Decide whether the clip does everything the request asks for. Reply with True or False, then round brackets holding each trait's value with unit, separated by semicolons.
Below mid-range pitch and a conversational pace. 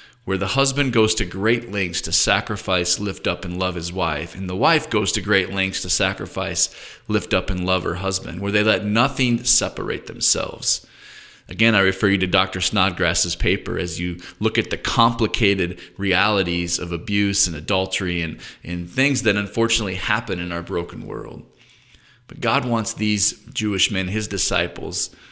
True (95 Hz; 175 wpm)